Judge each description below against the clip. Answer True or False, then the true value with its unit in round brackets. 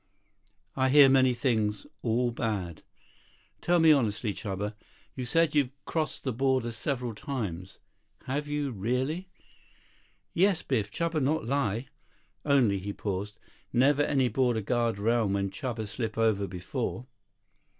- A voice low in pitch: True (120 Hz)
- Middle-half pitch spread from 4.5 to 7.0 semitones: True (4.9 semitones)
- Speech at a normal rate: False (130 wpm)